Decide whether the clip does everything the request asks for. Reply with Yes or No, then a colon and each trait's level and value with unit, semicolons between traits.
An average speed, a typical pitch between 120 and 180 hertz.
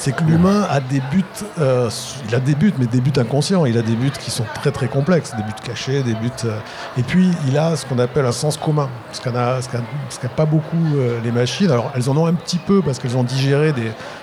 No: fast, 255 wpm; low, 135 Hz